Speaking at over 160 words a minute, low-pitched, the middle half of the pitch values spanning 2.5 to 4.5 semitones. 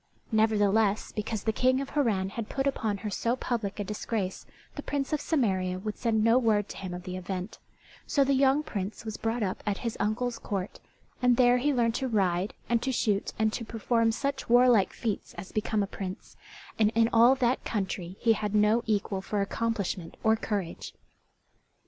No: average, 190 wpm; high, 220 Hz; average, 3.3 semitones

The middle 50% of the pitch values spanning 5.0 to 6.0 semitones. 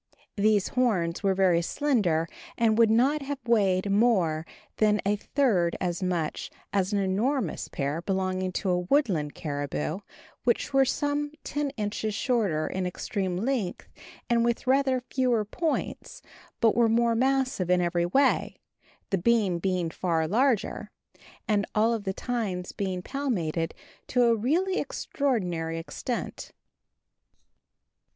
Yes: wide, 5.4 semitones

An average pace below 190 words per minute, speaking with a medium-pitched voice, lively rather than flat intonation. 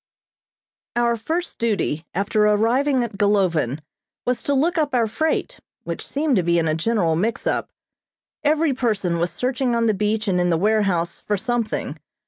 No: average, 170 wpm; high, 220 Hz; wide, 5.7 semitones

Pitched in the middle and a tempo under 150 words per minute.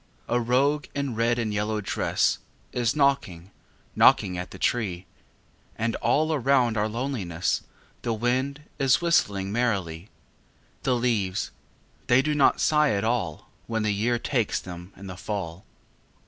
No: low, 115 Hz; average, 140 wpm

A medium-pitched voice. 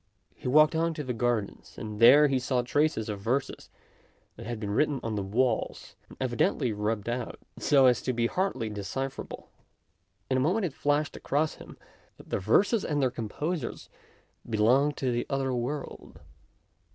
No: low, 130 Hz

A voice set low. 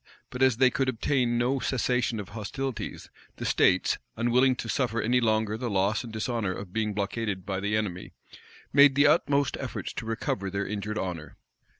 Yes: low, 115 Hz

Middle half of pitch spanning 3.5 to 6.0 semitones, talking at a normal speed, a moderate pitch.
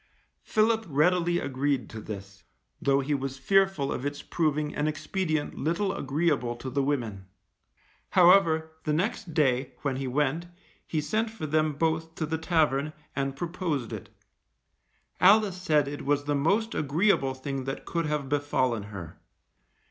Yes: average, 3.9 semitones; average, 150 wpm; medium, 150 Hz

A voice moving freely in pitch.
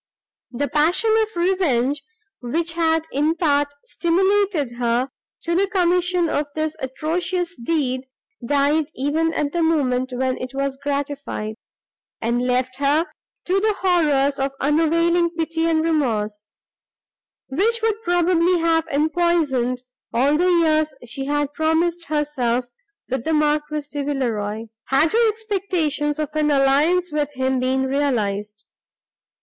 No: average, 4.2 semitones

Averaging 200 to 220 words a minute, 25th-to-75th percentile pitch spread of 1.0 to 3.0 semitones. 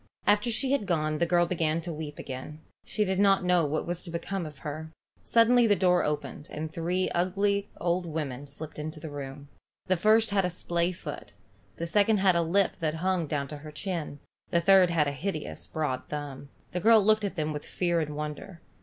No: fast, 205 wpm; average, 4.1 semitones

